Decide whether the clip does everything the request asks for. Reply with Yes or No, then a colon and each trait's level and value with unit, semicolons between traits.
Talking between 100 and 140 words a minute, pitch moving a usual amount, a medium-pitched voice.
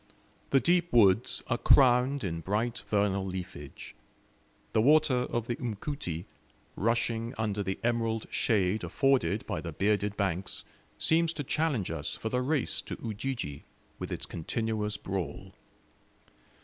No: slow, 135 wpm; average, 4.3 semitones; low, 110 Hz